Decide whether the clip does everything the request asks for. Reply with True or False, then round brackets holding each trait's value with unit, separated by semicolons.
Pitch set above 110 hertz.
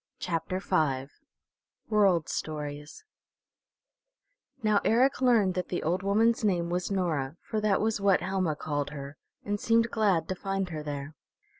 True (185 Hz)